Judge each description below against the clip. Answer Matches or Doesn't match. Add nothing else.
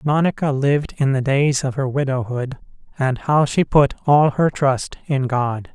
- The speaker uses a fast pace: Doesn't match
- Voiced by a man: Matches